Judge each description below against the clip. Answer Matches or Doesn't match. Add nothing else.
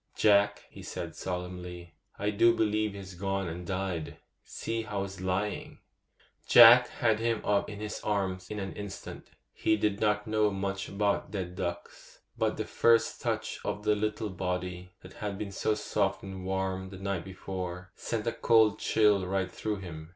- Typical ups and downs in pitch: Doesn't match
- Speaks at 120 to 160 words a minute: Doesn't match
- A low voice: Matches